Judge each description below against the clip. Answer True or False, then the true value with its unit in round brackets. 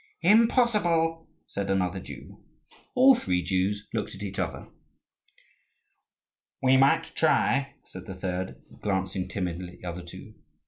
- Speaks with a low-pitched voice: True (100 Hz)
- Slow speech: True (130 wpm)